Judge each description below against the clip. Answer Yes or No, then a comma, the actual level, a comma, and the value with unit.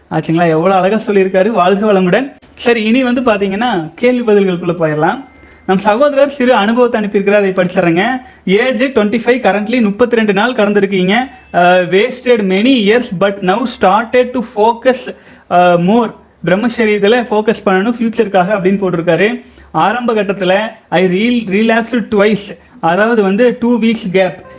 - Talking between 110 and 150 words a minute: Yes, fast, 130 wpm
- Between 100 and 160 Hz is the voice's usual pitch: No, high, 210 Hz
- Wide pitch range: No, average, 4.1 semitones